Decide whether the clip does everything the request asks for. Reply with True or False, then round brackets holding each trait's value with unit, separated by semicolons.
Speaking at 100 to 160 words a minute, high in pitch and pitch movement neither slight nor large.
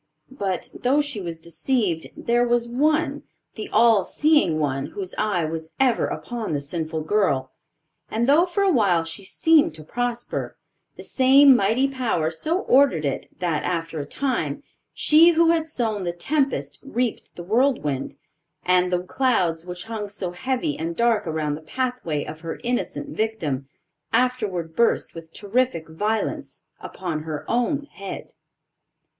False (150 wpm; 210 Hz; 7.7 semitones)